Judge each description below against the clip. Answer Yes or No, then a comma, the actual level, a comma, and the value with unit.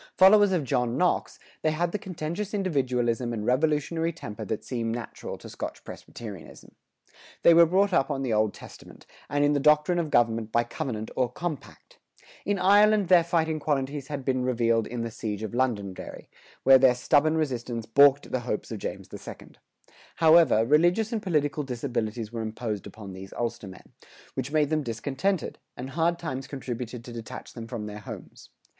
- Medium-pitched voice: No, low, 130 Hz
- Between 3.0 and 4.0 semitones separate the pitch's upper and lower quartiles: No, wide, 5.6 semitones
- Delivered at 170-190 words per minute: Yes, average, 175 wpm